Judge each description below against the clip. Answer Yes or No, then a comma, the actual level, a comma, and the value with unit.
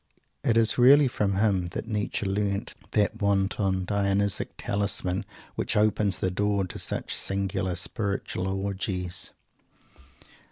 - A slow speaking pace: Yes, slow, 120 wpm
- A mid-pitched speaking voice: No, low, 100 Hz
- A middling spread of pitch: No, narrow, 1.5 semitones